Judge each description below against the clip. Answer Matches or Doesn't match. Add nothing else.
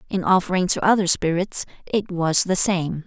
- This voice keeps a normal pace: Matches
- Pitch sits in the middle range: Matches